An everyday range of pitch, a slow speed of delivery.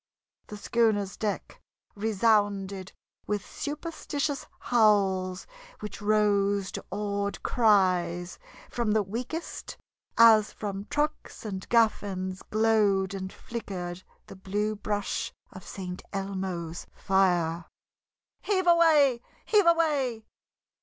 Yes: average, 3.3 semitones; slow, 100 wpm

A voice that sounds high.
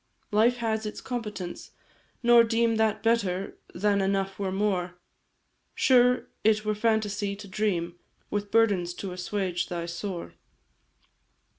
Yes: high, 205 Hz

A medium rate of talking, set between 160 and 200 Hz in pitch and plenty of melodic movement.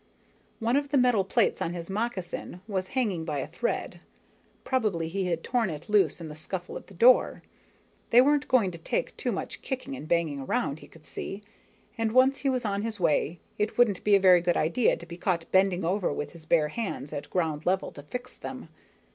No: fast, 215 wpm; high, 190 Hz; wide, 5.8 semitones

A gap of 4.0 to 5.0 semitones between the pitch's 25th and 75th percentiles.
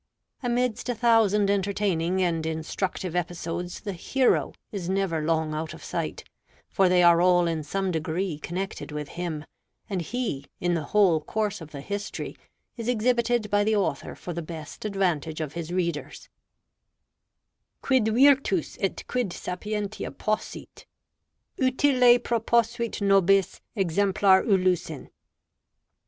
Yes: average, 4.3 semitones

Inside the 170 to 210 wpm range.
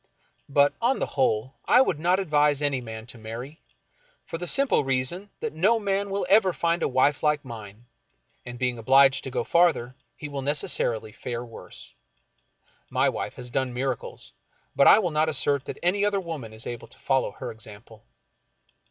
Yes: average, 180 wpm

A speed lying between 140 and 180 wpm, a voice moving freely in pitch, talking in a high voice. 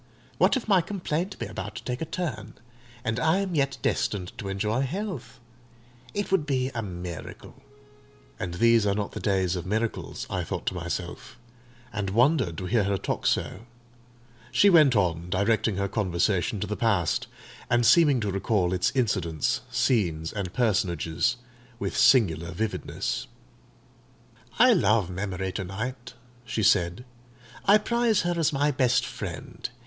No: average, 155 wpm; wide, 6.0 semitones; low, 110 Hz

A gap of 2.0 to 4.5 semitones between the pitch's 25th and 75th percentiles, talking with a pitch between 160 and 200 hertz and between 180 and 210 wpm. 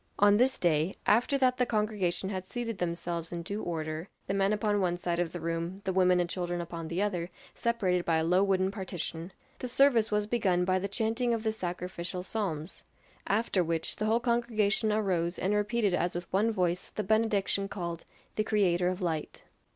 Yes: average, 3.6 semitones; high, 190 Hz; average, 195 wpm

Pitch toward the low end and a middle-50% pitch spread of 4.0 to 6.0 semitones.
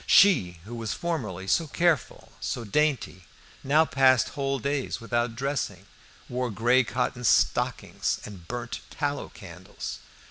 Yes: low, 125 Hz; average, 4.5 semitones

